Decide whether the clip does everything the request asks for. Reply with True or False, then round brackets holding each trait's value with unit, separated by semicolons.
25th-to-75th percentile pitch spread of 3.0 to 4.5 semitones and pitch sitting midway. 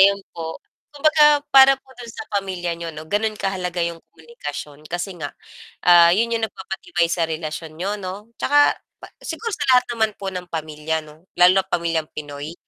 False (5.3 semitones; 180 Hz)